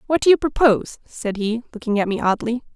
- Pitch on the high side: Yes, high, 235 Hz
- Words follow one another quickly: Yes, fast, 220 wpm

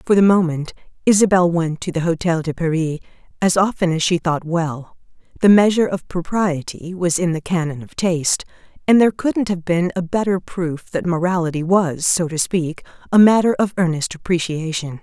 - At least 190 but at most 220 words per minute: No, average, 180 wpm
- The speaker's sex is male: No, female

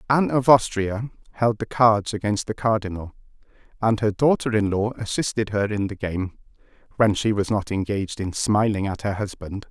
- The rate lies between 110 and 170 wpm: No, average, 180 wpm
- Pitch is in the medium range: No, low, 105 Hz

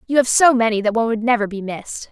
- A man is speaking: No, female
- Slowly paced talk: No, fast, 285 wpm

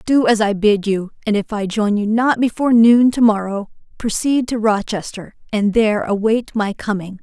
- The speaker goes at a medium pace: Yes, average, 190 wpm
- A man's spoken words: No, female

